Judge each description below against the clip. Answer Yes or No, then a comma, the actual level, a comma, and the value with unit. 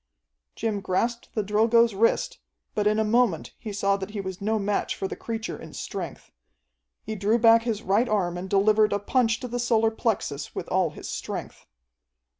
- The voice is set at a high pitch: Yes, high, 215 Hz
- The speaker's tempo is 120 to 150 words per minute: No, average, 190 wpm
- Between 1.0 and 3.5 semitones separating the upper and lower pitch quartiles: Yes, narrow, 2.4 semitones